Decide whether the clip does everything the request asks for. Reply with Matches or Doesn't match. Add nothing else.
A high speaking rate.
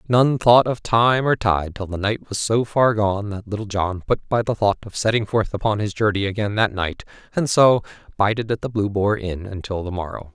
Matches